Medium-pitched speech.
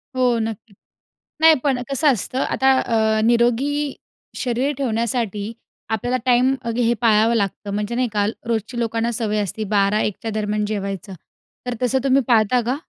No: high, 230 Hz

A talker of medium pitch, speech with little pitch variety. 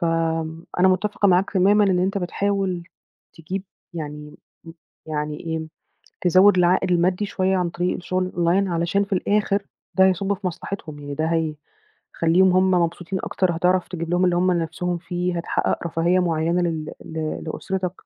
Yes: medium, 180 Hz; narrow, 2.3 semitones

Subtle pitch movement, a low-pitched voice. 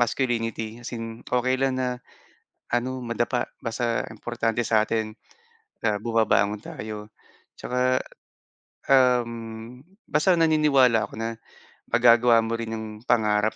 Yes: narrow, 2.0 semitones; low, 115 Hz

